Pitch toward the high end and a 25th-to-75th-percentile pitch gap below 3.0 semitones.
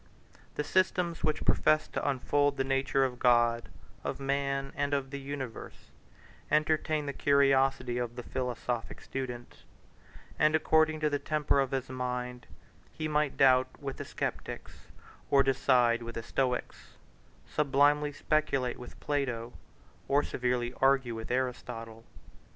No: low, 135 Hz; narrow, 2.6 semitones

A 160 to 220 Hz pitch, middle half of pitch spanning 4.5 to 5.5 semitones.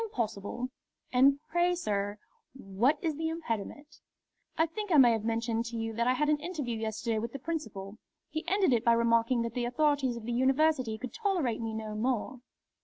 No: high, 245 Hz; average, 5.1 semitones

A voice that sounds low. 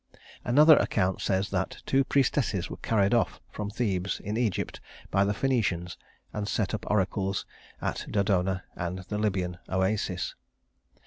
Yes: low, 100 Hz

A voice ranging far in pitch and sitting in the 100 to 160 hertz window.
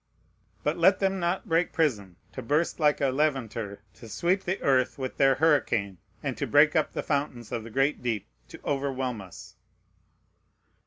Yes: wide, 5.7 semitones; low, 135 Hz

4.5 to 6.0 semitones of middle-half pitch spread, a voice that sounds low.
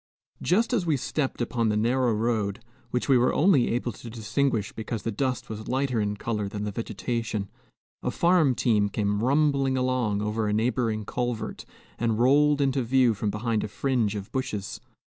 No: average, 3.6 semitones; low, 120 Hz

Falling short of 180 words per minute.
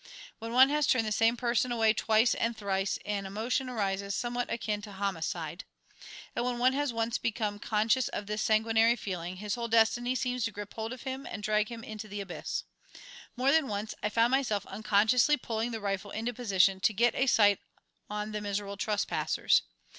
No: average, 190 wpm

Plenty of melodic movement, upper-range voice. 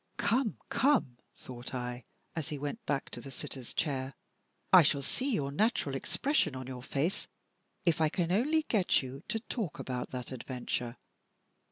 No: wide, 7.8 semitones; medium, 140 Hz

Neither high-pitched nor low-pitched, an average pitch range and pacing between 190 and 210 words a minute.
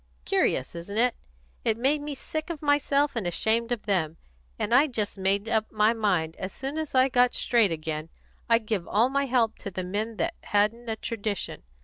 No: high, 225 Hz; average, 4.4 semitones; average, 200 wpm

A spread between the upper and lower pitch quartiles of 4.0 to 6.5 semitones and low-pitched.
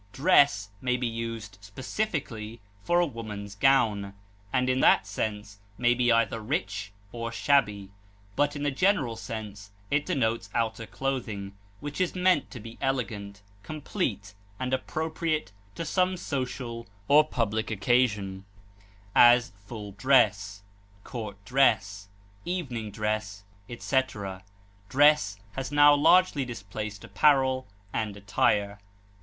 Yes: average, 5.0 semitones; low, 115 Hz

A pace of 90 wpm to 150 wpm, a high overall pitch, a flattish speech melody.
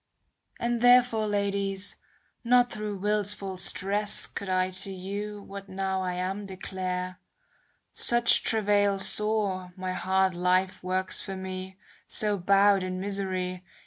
Yes: slow, 135 wpm; high, 195 Hz; narrow, 1.8 semitones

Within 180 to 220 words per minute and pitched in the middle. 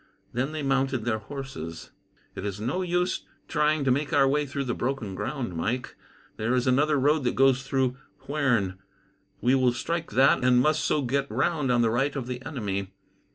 No: average, 190 wpm; low, 130 Hz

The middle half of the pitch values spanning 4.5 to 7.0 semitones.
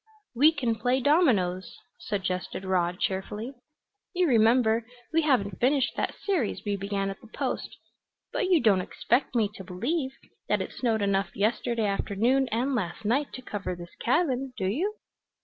Yes: average, 5.1 semitones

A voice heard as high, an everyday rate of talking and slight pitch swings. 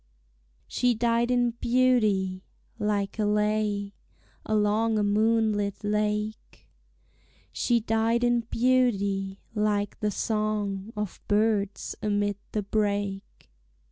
No: high, 210 Hz; slow, 100 wpm; narrow, 1.8 semitones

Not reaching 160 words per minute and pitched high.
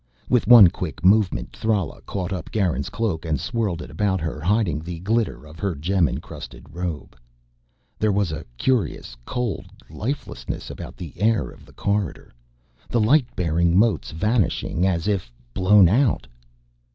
No: average, 150 wpm; very low, 95 Hz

